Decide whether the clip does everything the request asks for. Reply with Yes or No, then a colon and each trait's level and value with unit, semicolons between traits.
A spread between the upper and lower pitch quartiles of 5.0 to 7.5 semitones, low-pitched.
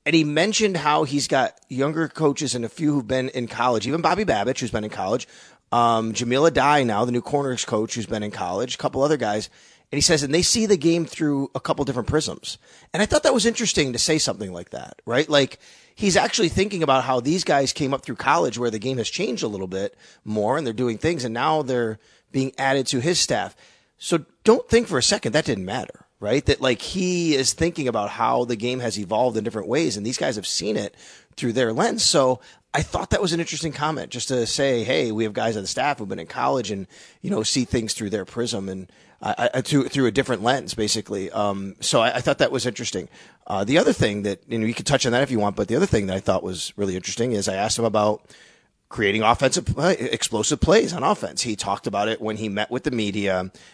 Yes: wide, 5.5 semitones; low, 130 Hz